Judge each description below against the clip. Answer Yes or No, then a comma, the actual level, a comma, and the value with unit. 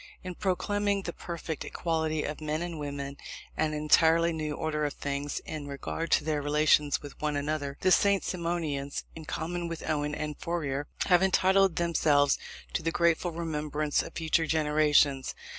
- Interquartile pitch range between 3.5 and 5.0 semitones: No, narrow, 2.5 semitones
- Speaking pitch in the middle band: Yes, medium, 155 Hz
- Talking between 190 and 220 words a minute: No, average, 165 wpm